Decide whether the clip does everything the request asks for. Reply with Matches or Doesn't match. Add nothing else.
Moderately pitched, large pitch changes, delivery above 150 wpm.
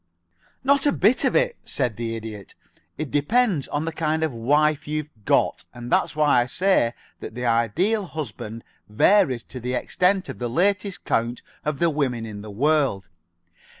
Matches